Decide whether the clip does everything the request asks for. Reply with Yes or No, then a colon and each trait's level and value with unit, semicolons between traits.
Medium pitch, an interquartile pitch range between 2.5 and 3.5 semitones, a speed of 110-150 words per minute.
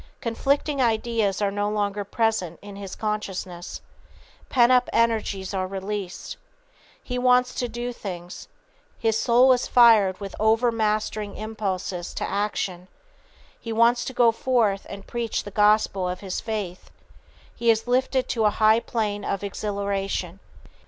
No: high, 215 Hz; average, 2.9 semitones; average, 140 wpm